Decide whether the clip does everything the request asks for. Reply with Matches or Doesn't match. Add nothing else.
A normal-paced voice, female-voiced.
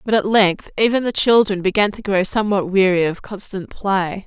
Matches